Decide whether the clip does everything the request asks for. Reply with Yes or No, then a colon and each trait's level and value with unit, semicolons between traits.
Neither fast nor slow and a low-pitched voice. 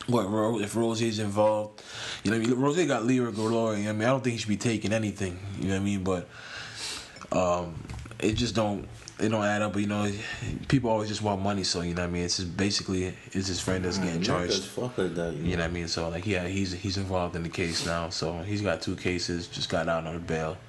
No: fast, 250 wpm; low, 100 Hz